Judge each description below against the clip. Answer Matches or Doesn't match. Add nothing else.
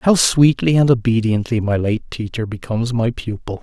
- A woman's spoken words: Doesn't match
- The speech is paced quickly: Doesn't match